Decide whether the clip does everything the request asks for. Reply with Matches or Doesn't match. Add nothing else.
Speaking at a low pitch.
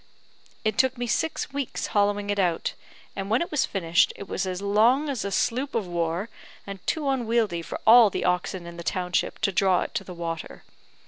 Doesn't match